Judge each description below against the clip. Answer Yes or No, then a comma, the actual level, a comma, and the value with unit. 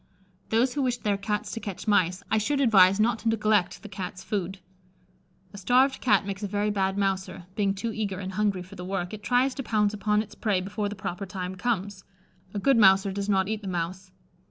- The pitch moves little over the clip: Yes, narrow, 2.2 semitones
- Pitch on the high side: Yes, high, 200 Hz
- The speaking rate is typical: No, fast, 220 wpm